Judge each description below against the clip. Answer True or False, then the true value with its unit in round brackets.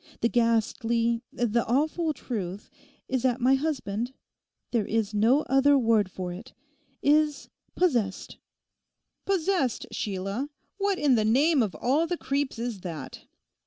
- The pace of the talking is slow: True (120 wpm)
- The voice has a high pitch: True (245 Hz)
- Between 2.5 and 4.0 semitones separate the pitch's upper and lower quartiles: False (4.8 semitones)